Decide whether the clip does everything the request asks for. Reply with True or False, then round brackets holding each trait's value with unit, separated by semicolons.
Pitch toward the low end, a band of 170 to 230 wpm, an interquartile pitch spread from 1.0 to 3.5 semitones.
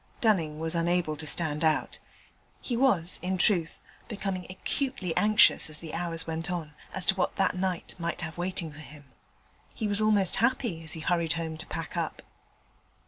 False (175 Hz; 180 wpm; 3.1 semitones)